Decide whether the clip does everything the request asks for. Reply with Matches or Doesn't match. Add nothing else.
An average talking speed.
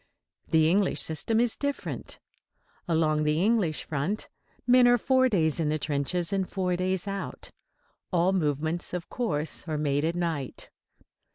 Matches